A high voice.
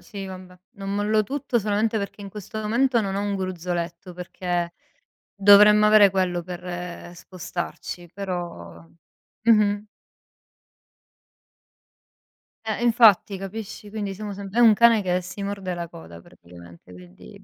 Yes: high, 195 Hz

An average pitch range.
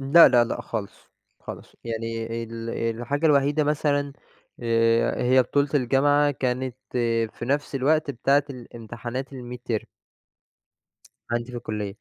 Yes: average, 3.5 semitones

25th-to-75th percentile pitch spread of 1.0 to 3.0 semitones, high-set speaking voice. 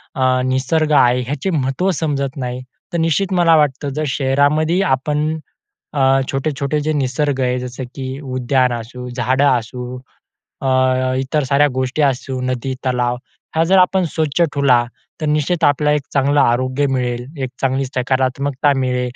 No: narrow, 2.5 semitones; low, 135 Hz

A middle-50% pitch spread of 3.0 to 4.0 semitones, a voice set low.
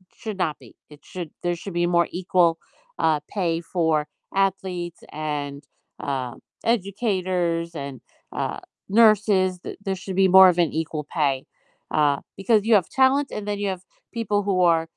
No: average, 3.3 semitones; medium, 180 Hz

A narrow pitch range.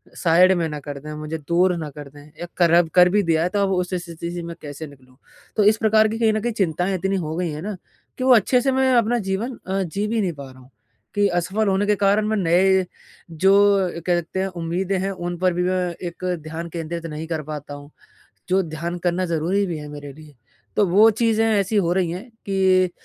No: average, 3.7 semitones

